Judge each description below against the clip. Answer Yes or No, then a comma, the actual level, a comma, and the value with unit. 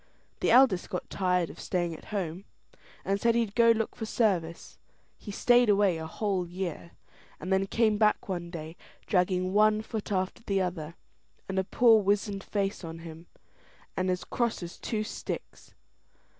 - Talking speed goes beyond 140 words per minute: Yes, average, 170 wpm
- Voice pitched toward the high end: Yes, high, 195 Hz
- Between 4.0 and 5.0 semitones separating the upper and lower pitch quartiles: No, average, 3.3 semitones